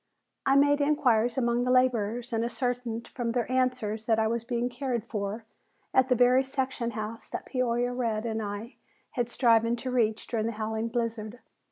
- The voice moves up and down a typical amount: No, narrow, 2.1 semitones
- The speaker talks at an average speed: Yes, average, 180 wpm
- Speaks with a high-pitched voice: Yes, high, 235 Hz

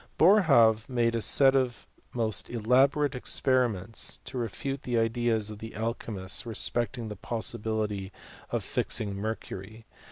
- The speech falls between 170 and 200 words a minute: No, slow, 135 wpm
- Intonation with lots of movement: No, narrow, 2.5 semitones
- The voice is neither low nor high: No, low, 115 Hz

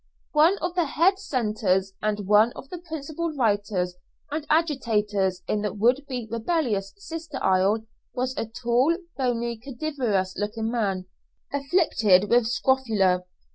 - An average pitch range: No, wide, 5.9 semitones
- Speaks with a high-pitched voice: Yes, high, 235 Hz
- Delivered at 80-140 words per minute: Yes, slow, 135 wpm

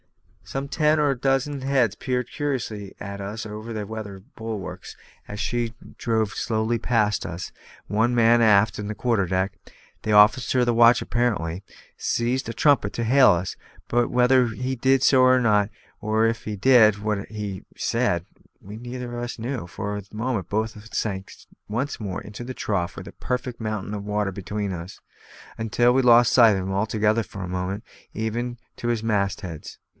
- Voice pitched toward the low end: Yes, low, 110 Hz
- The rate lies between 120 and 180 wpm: No, average, 190 wpm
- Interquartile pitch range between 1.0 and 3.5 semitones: Yes, average, 3.0 semitones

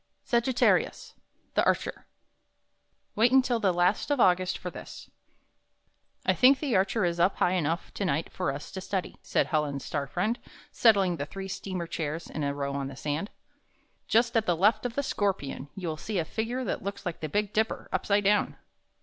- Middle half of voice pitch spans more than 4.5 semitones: Yes, average, 5.2 semitones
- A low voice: No, high, 190 Hz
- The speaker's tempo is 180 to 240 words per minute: Yes, average, 190 wpm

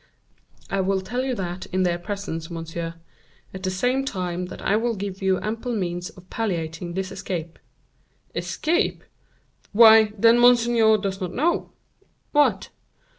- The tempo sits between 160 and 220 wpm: No, average, 145 wpm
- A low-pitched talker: No, high, 195 Hz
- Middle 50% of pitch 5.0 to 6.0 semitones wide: No, average, 4.2 semitones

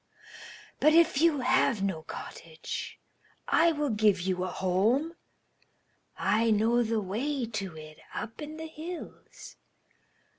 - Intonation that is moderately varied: No, wide, 7.6 semitones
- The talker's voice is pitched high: Yes, high, 230 Hz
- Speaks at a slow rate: Yes, slow, 125 wpm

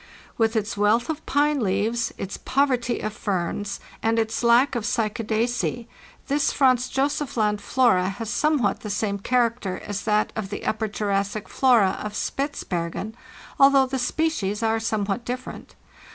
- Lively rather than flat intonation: No, average, 3.6 semitones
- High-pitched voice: Yes, high, 225 Hz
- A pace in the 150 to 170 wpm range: Yes, average, 155 wpm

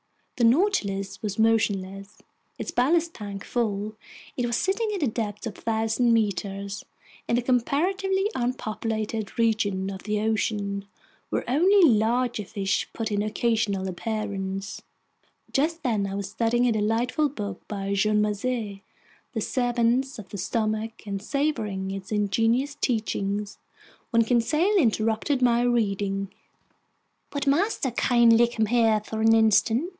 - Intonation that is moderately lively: Yes, average, 3.3 semitones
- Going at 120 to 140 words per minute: Yes, slow, 135 wpm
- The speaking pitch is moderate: No, high, 225 Hz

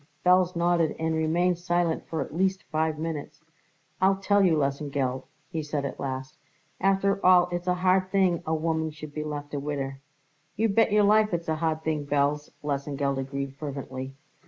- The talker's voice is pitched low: No, medium, 160 Hz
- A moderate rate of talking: Yes, average, 180 wpm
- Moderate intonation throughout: Yes, average, 4.0 semitones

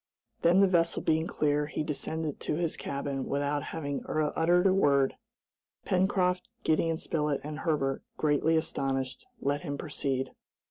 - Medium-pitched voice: Yes, medium, 150 Hz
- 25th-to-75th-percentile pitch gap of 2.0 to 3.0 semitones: Yes, narrow, 2.6 semitones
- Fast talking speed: No, average, 140 wpm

